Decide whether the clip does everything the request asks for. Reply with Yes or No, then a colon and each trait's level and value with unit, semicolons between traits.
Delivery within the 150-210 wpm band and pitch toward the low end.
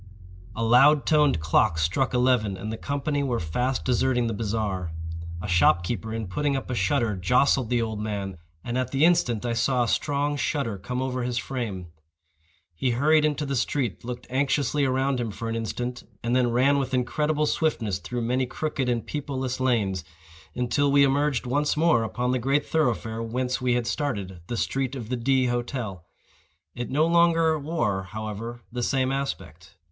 Yes: average, 180 wpm; low, 125 Hz